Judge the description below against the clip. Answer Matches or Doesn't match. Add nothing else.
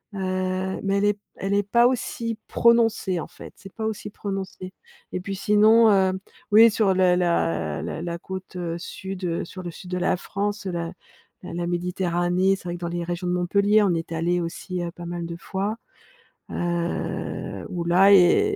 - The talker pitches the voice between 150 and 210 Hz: Matches